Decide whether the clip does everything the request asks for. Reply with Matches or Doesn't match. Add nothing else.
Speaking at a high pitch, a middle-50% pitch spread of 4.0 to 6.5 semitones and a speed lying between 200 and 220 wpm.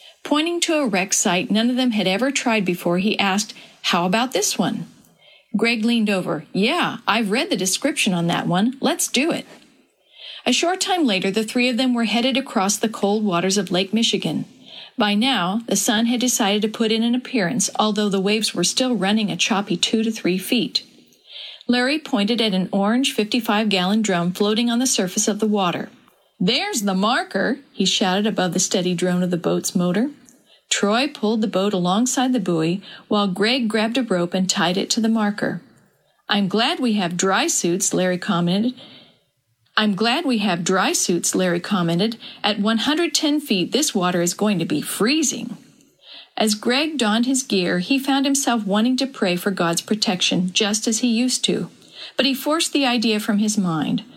Doesn't match